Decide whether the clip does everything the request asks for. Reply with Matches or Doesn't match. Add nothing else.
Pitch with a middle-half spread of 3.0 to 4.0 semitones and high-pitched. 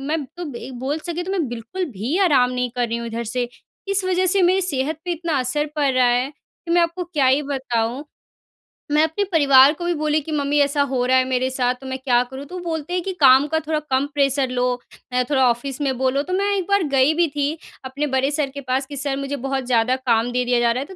Matches